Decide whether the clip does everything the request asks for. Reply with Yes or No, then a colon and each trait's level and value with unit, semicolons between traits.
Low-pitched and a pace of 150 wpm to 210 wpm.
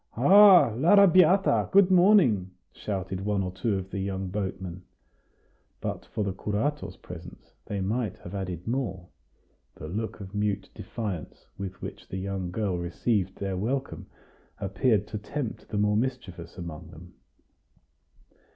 No: low, 100 Hz; average, 140 wpm